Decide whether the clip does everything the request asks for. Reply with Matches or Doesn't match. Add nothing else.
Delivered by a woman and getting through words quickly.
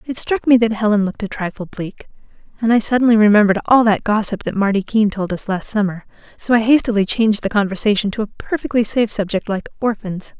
Matches